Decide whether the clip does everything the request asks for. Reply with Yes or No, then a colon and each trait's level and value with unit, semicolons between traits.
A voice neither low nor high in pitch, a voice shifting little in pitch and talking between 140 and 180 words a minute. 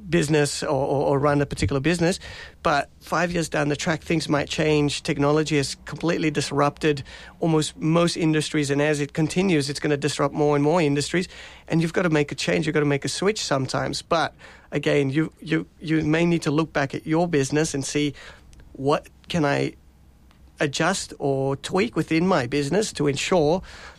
No: medium, 150 Hz; narrow, 2.2 semitones; average, 190 wpm